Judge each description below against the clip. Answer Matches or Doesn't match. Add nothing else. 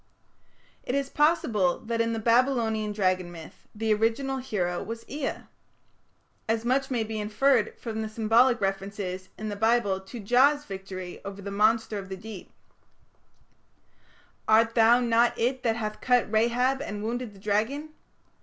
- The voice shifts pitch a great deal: Doesn't match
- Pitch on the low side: Doesn't match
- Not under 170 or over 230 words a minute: Doesn't match